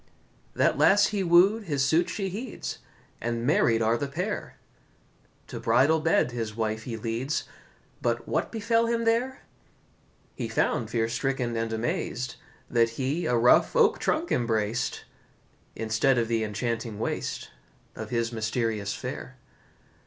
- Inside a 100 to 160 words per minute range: Yes, average, 140 wpm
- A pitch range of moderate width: No, wide, 7.1 semitones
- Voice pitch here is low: Yes, low, 120 Hz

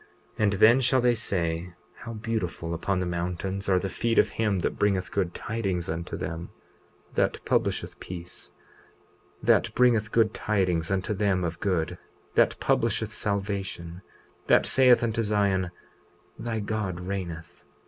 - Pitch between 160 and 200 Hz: No, very low, 95 Hz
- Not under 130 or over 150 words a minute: Yes, average, 145 wpm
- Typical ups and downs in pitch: Yes, average, 3.5 semitones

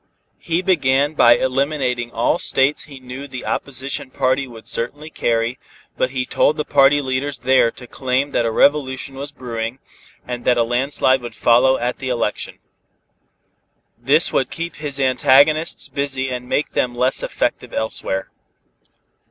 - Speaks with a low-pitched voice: Yes, low, 130 Hz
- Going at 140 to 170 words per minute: Yes, average, 150 wpm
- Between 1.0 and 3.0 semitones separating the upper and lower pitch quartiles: Yes, narrow, 2.4 semitones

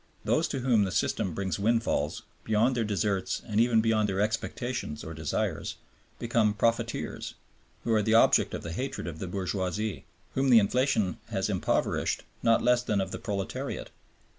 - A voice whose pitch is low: Yes, low, 105 Hz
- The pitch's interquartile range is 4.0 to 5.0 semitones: No, average, 3.4 semitones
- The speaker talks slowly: No, average, 165 wpm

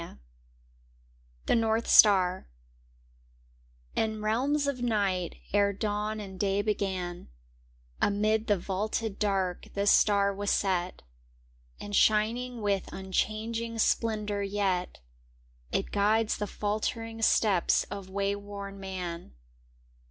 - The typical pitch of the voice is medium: No, high, 205 Hz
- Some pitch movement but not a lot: No, narrow, 2.0 semitones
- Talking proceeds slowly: Yes, slow, 105 wpm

